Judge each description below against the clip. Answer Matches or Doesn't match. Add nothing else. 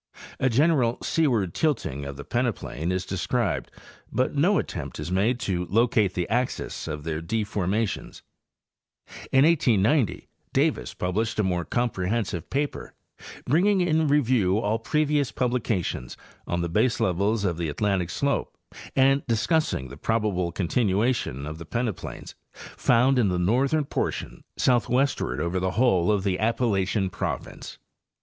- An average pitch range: Doesn't match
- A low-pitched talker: Matches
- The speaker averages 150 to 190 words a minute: Doesn't match